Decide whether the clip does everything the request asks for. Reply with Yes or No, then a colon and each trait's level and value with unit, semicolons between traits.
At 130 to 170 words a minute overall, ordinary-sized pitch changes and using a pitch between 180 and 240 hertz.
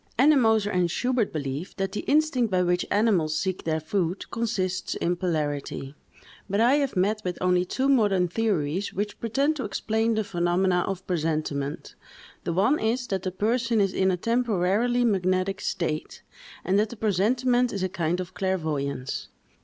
Yes: average, 165 wpm; average, 4.3 semitones; high, 190 Hz